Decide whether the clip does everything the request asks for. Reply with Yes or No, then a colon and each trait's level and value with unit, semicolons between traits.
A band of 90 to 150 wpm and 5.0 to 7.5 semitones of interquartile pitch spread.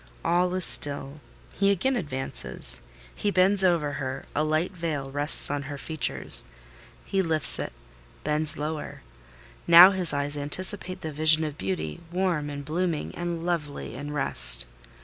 No: average, 145 wpm; average, 3.7 semitones